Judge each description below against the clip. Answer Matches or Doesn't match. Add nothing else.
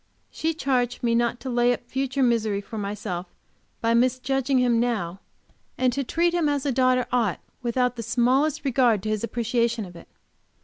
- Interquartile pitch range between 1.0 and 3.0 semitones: Matches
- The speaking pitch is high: Matches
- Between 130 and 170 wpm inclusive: Doesn't match